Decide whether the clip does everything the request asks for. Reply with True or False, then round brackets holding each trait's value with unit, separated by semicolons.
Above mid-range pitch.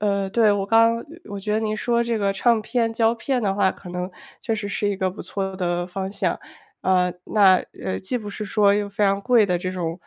True (200 Hz)